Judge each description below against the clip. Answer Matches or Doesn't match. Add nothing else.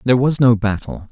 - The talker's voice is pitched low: Matches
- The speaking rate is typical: Doesn't match